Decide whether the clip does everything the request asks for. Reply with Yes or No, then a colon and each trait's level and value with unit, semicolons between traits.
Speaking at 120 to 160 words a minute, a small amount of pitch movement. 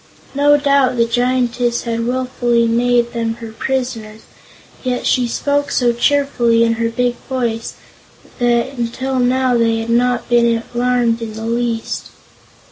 Yes: average, 140 wpm; narrow, 1.6 semitones